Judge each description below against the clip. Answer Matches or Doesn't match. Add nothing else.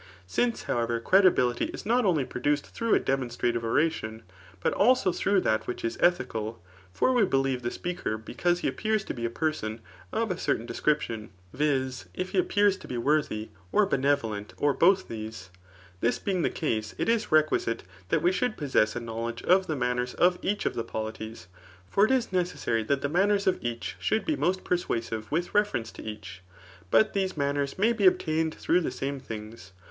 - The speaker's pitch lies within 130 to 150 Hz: Matches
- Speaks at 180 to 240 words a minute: Matches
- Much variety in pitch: Matches